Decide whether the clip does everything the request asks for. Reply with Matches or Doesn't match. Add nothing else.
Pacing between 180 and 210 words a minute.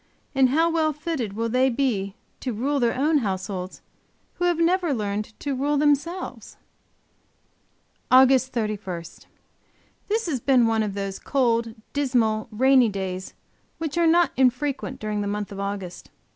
Doesn't match